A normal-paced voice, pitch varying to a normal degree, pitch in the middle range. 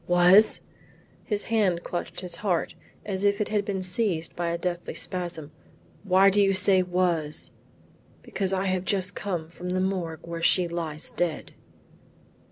No: average, 160 wpm; narrow, 2.3 semitones; medium, 180 Hz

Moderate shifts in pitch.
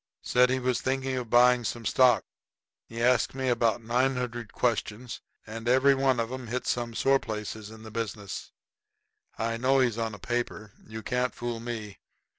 No: narrow, 2.0 semitones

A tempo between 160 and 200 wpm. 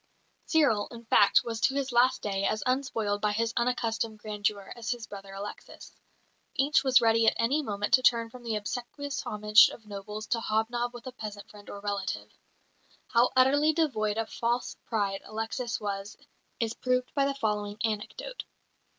Yes: average, 170 wpm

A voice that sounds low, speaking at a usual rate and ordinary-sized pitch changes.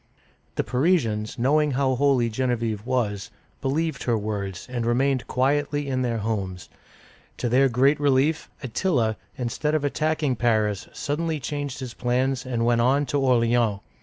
Yes: low, 125 Hz; average, 145 wpm; average, 3.5 semitones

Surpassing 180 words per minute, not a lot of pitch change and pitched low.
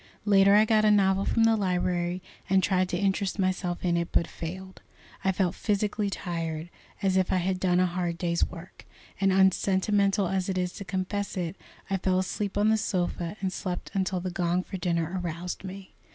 No: average, 195 wpm; narrow, 1.8 semitones; medium, 185 Hz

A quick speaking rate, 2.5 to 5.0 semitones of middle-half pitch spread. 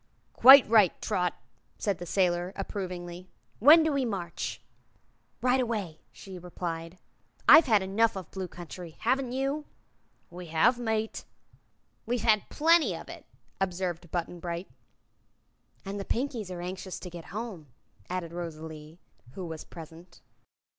No: average, 140 wpm; average, 4.6 semitones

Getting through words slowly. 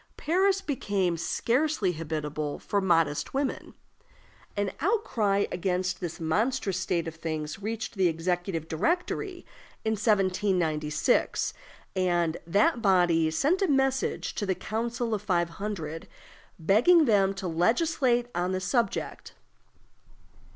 Yes: slow, 115 wpm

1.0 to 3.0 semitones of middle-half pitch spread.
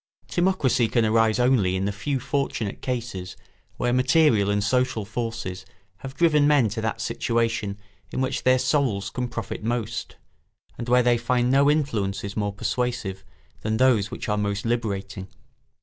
No: average, 3.8 semitones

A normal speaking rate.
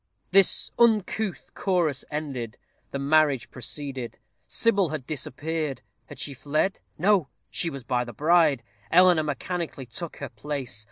No: slow, 130 wpm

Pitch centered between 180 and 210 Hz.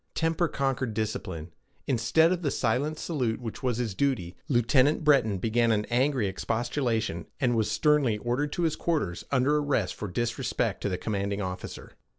No: low, 120 Hz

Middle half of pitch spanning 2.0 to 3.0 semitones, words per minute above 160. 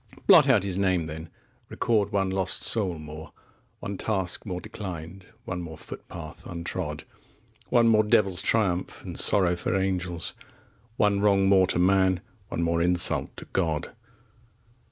No: narrow, 2.5 semitones; average, 150 wpm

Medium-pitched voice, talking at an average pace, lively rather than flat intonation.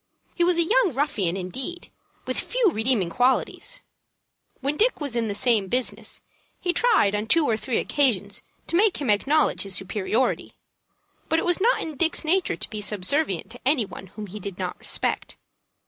No: very high, 255 Hz; average, 180 wpm; wide, 8.2 semitones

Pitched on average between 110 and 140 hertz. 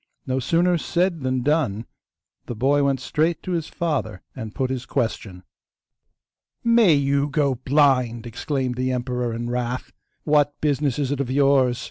Yes: low, 135 Hz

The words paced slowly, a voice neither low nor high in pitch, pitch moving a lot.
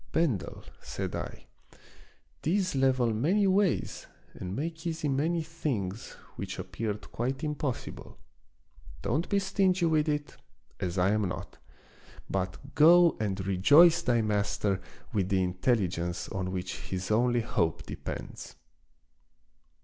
No: slow, 125 wpm; low, 125 Hz; wide, 8.8 semitones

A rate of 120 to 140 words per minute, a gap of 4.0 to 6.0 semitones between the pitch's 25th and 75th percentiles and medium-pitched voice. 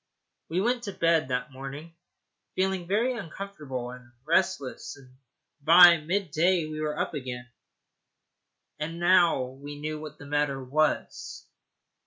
Yes: slow, 135 wpm; average, 4.4 semitones; medium, 155 Hz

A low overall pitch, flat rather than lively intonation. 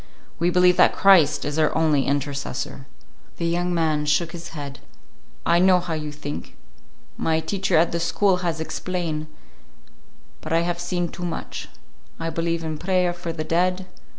No: medium, 170 Hz; narrow, 2.2 semitones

